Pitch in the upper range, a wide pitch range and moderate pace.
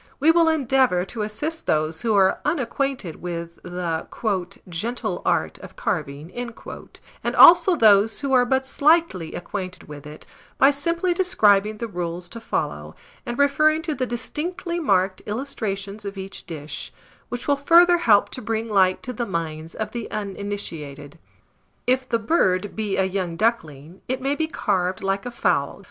Yes: high, 215 Hz; wide, 7.1 semitones; average, 160 wpm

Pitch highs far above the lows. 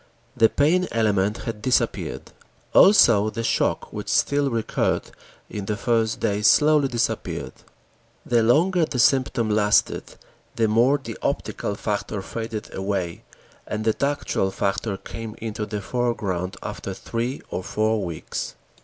No: average, 2.9 semitones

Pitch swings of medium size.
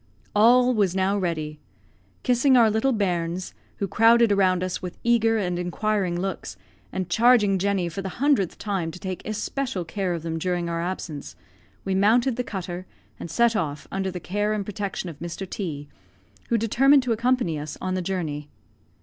Yes: average, 4.2 semitones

